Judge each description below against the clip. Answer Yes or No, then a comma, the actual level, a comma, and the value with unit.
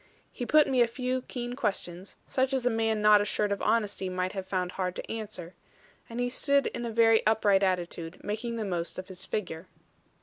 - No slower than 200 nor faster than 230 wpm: Yes, fast, 205 wpm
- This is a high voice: Yes, high, 210 Hz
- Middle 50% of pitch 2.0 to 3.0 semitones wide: No, average, 4.3 semitones